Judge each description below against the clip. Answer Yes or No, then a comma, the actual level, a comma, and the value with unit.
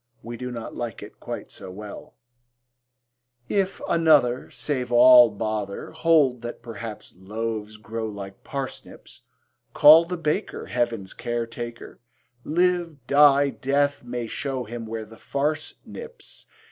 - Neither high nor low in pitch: No, low, 120 Hz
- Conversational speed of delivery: No, slow, 130 wpm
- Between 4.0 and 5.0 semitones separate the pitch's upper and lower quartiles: Yes, average, 4.3 semitones